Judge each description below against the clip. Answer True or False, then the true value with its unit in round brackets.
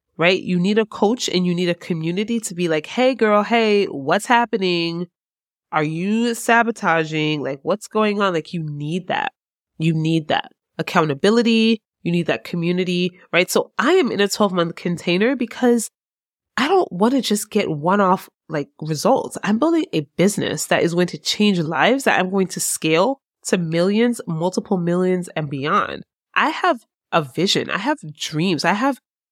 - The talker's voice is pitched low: False (185 Hz)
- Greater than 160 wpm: True (180 wpm)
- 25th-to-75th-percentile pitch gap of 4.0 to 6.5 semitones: True (5.0 semitones)